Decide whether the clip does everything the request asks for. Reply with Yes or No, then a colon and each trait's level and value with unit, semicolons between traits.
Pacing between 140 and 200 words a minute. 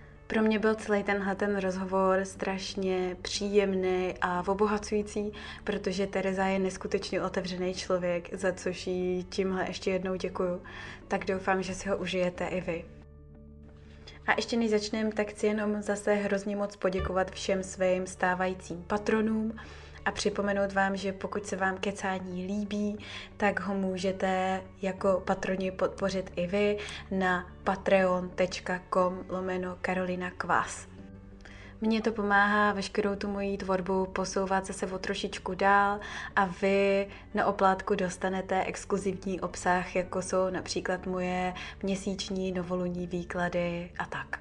No: average, 130 wpm